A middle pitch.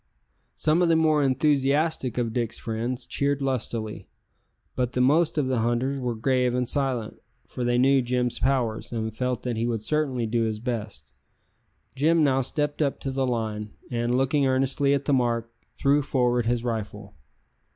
No: low, 125 Hz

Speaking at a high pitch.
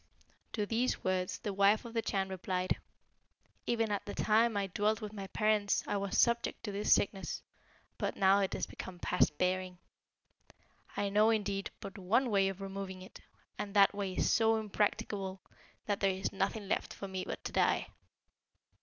Yes: high, 200 Hz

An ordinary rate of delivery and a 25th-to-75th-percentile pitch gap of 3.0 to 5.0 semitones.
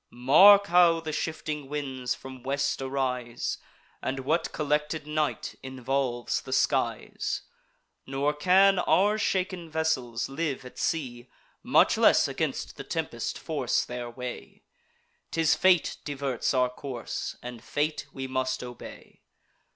No: slow, 125 wpm; average, 3.8 semitones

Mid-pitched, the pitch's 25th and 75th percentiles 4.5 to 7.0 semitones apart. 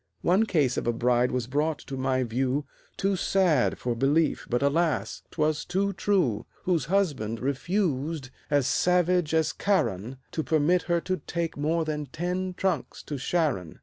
Yes: medium, 155 Hz; average, 5.2 semitones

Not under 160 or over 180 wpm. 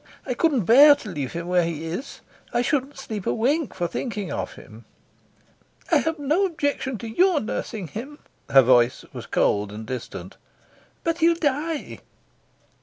Yes: average, 165 wpm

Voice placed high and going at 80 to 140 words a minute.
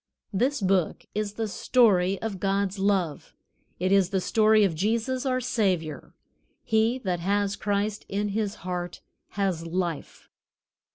Yes: high, 200 Hz; slow, 135 wpm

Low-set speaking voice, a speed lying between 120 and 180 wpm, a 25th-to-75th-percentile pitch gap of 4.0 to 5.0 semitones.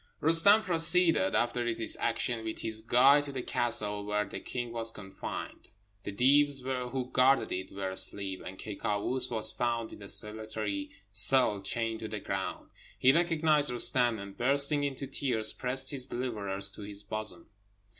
Yes: low, 115 Hz; average, 165 wpm; average, 4.4 semitones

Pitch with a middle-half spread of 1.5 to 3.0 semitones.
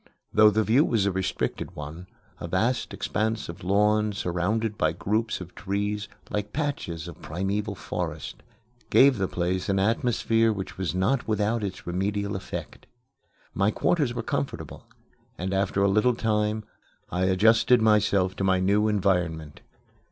Yes: average, 2.7 semitones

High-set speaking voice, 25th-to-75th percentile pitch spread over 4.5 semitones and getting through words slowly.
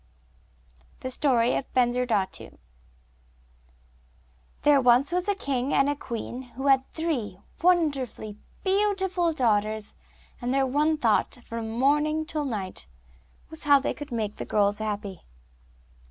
Yes: very high, 255 Hz; wide, 5.5 semitones; slow, 130 wpm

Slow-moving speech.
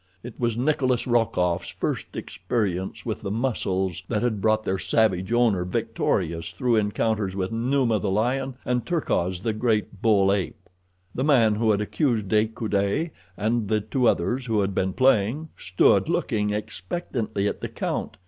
No: average, 160 wpm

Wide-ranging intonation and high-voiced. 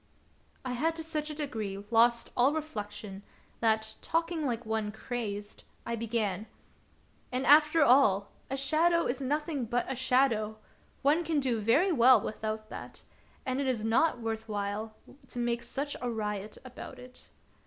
No: average, 4.5 semitones; high, 245 Hz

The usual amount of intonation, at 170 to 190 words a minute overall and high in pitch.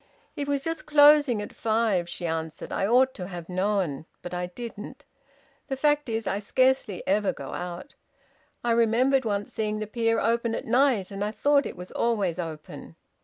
No: wide, 5.9 semitones; average, 180 wpm; high, 220 Hz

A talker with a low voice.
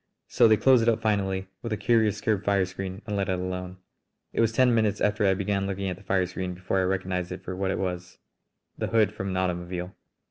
Yes: very low, 95 Hz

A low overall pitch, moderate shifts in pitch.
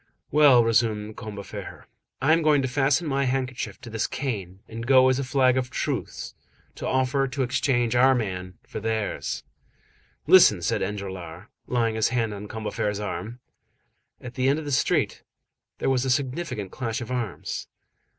Yes: low, 125 Hz; average, 3.5 semitones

